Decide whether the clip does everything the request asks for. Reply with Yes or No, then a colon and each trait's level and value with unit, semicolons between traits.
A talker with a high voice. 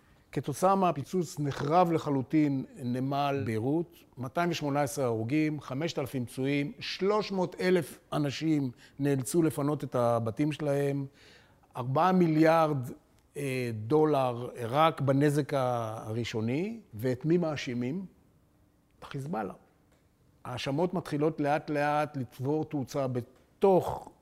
No: medium, 145 Hz